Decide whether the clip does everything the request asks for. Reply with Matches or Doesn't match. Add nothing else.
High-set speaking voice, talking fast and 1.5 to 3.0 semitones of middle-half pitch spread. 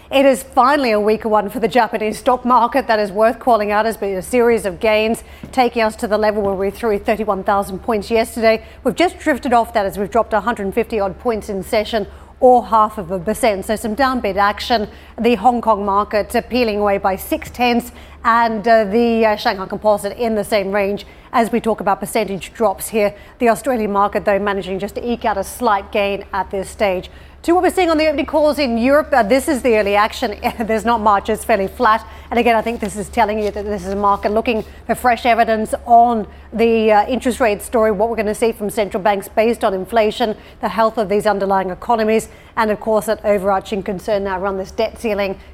Matches